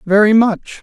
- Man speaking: Yes, male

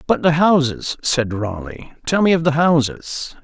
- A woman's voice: No, male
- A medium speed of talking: Yes, average, 175 wpm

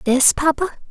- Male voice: No, female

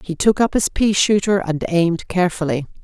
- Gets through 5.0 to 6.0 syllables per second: Yes, 5.5 syllables/s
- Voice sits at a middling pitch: Yes, medium, 180 Hz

